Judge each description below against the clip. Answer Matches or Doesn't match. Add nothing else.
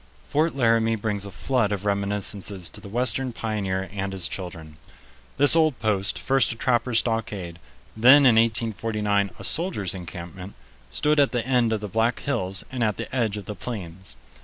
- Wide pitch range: Doesn't match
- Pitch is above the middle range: Doesn't match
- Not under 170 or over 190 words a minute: Matches